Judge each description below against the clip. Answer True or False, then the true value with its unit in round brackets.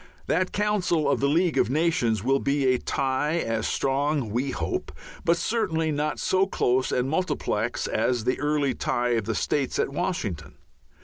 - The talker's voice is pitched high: False (140 Hz)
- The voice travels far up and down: False (4.7 semitones)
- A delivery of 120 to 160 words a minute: False (170 wpm)